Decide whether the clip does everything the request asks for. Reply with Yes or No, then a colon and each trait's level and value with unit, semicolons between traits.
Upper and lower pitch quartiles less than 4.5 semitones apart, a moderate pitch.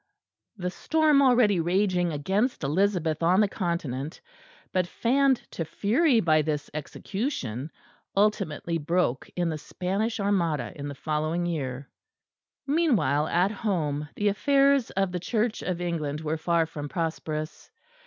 No: average, 5.2 semitones; medium, 175 Hz